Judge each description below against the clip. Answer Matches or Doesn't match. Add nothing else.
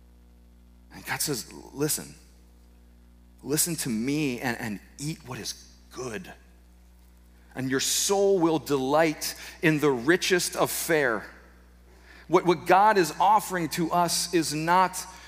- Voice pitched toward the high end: Doesn't match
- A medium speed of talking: Doesn't match